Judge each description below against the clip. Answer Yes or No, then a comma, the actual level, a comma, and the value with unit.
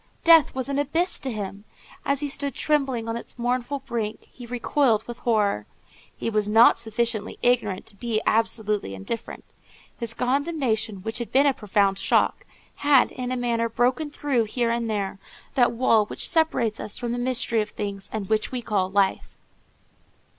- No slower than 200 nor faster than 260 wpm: No, average, 175 wpm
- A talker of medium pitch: No, high, 235 Hz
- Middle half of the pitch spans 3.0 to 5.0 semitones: Yes, average, 3.3 semitones